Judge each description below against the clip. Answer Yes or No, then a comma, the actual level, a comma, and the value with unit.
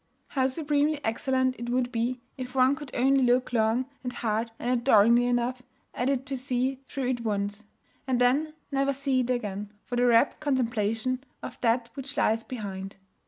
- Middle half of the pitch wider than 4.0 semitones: No, narrow, 2.4 semitones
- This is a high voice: Yes, very high, 250 Hz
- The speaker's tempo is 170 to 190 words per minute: Yes, average, 175 wpm